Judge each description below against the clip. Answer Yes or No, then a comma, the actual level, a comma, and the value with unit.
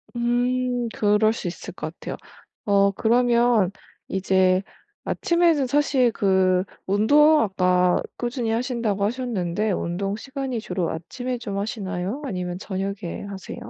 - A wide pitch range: No, average, 4.5 semitones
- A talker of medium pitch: No, high, 215 Hz